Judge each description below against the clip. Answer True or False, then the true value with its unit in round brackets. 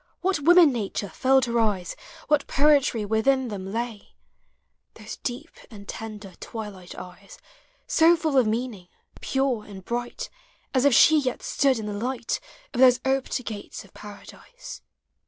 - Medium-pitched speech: False (240 Hz)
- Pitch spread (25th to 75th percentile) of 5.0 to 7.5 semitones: False (4.5 semitones)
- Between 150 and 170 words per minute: True (165 wpm)